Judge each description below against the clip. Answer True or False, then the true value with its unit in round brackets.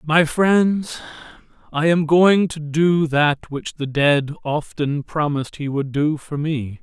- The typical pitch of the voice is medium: True (155 Hz)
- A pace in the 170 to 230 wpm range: False (160 wpm)